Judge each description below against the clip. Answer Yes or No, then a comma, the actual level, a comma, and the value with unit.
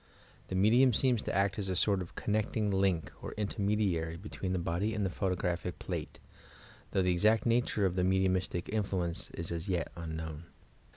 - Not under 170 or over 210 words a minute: Yes, average, 180 wpm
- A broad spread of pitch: No, average, 3.1 semitones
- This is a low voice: Yes, very low, 95 Hz